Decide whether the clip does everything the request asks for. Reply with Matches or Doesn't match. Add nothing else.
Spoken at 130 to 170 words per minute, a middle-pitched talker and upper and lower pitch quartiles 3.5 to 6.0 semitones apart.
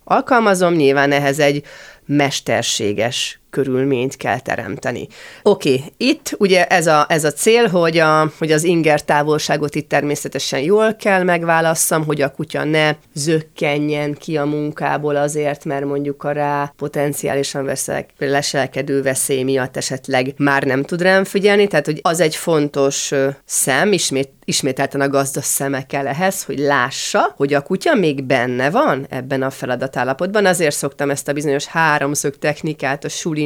Doesn't match